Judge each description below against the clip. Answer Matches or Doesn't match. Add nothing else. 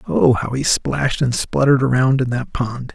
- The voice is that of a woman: Doesn't match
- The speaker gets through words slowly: Doesn't match